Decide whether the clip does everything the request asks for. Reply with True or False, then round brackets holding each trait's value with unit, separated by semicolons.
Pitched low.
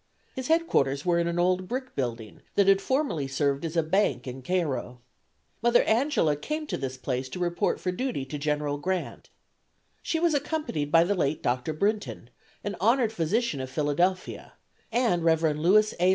False (170 Hz)